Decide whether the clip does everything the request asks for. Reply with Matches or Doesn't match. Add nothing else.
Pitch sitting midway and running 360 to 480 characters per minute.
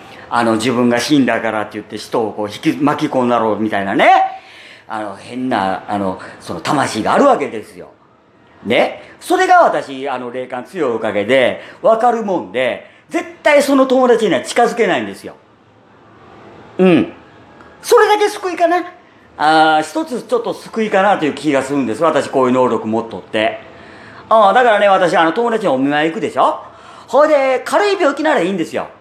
Doesn't match